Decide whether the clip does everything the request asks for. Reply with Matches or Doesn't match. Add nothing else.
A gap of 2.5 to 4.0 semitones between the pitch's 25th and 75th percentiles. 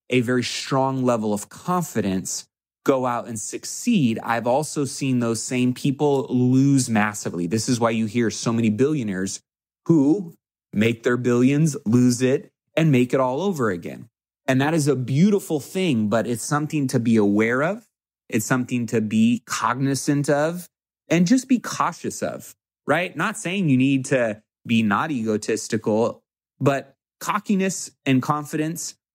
Doesn't match